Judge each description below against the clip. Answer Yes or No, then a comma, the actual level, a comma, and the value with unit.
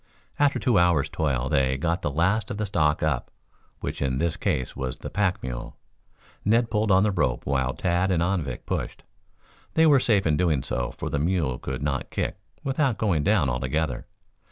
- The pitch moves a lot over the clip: Yes, wide, 6.8 semitones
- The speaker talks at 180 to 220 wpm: Yes, average, 190 wpm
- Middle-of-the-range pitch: No, very low, 80 Hz